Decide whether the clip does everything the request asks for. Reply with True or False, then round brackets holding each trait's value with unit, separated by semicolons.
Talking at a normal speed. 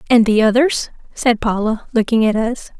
True (170 wpm)